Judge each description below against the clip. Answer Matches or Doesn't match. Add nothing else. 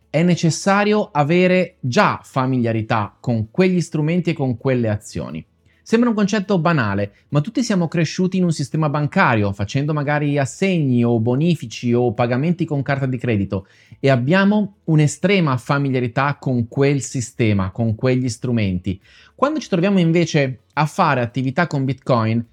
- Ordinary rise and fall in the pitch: Doesn't match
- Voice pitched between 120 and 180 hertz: Matches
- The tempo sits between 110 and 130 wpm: Doesn't match